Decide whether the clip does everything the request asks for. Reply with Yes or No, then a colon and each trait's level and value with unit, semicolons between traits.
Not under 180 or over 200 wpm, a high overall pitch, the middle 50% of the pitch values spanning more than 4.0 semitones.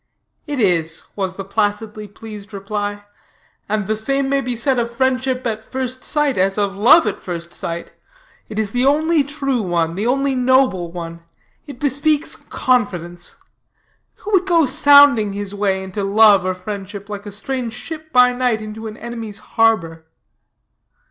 No: average, 160 wpm; high, 220 Hz; average, 4.8 semitones